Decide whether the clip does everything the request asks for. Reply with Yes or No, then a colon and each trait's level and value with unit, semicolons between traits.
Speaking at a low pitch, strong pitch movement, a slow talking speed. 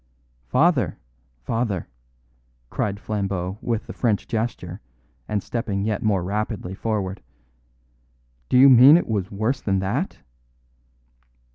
No: low, 105 Hz; average, 3.0 semitones; slow, 115 wpm